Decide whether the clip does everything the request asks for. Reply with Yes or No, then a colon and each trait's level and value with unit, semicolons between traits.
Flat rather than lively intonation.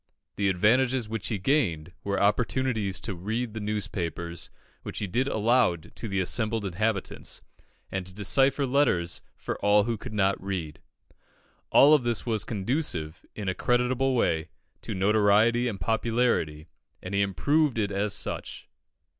No: average, 4.2 semitones